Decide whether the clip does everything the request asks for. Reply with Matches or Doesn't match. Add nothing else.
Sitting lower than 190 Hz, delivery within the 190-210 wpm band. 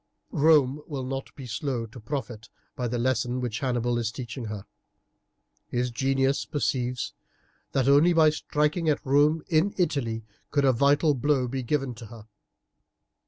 Doesn't match